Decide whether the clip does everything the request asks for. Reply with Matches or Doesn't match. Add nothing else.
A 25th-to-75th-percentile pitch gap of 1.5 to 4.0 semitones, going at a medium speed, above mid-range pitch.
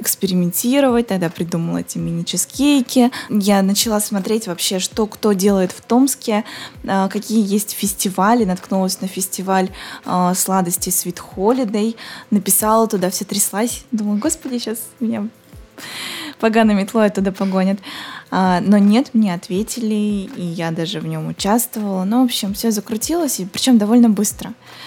Matches